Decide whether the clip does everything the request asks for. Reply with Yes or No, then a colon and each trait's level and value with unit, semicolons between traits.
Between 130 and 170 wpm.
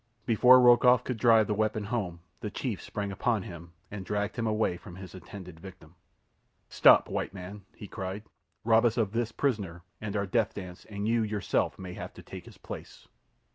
No: average, 190 wpm